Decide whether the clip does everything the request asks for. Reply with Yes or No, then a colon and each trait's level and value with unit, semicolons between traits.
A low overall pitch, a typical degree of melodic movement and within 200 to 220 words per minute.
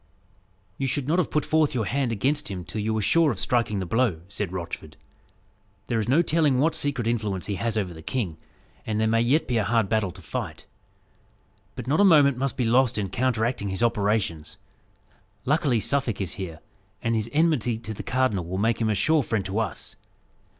Yes: low, 115 Hz; average, 4.5 semitones; fast, 205 wpm